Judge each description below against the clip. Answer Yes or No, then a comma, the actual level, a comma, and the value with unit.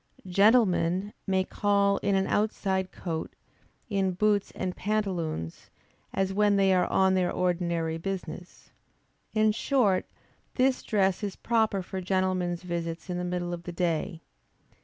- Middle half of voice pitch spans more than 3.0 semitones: No, narrow, 2.4 semitones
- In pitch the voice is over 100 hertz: Yes, high, 190 Hz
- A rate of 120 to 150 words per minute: Yes, average, 140 wpm